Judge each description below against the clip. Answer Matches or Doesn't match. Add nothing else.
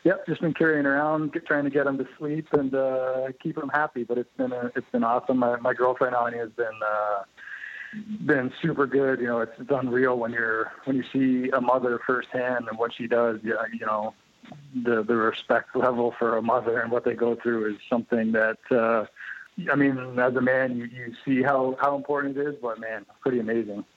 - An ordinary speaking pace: Doesn't match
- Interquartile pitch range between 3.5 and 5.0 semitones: Doesn't match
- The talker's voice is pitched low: Matches